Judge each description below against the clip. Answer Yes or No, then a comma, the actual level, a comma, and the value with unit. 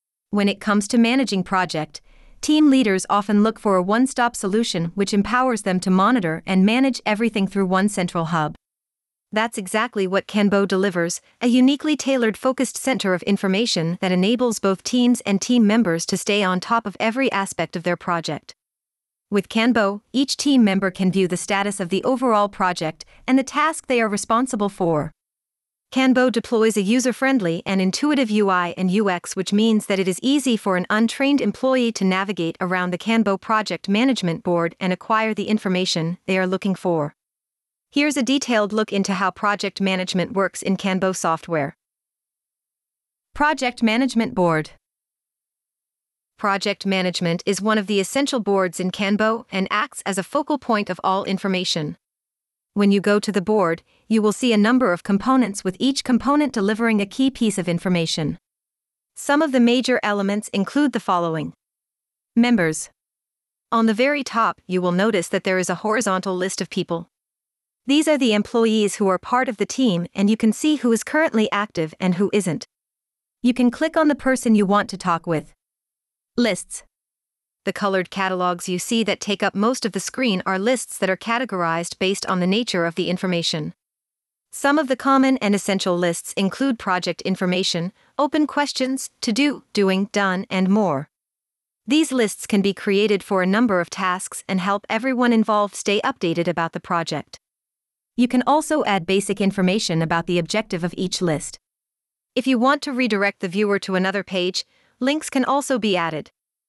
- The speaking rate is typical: Yes, average, 175 wpm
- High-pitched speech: Yes, high, 205 Hz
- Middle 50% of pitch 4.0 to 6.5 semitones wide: Yes, average, 4.3 semitones